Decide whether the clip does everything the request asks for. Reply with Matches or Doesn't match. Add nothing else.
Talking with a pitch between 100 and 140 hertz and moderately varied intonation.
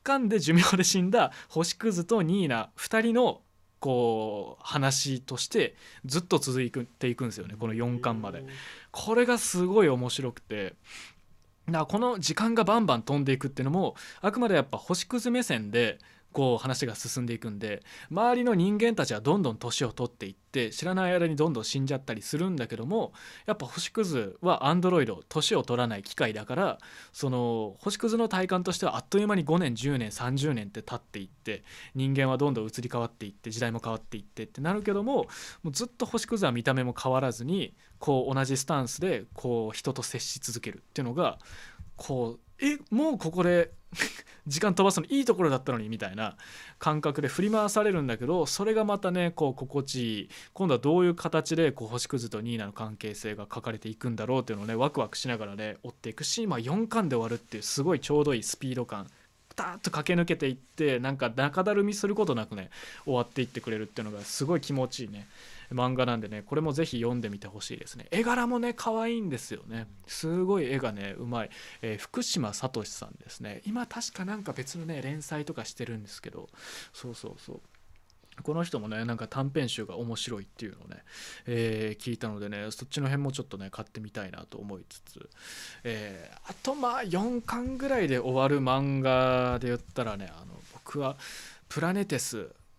Doesn't match